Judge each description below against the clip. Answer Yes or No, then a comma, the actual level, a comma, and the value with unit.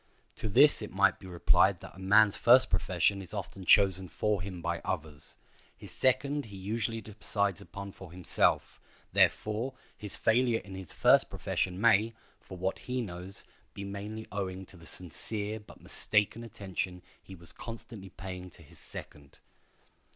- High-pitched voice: No, low, 100 Hz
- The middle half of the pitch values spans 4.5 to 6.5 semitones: No, average, 3.0 semitones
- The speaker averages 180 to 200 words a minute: No, average, 160 wpm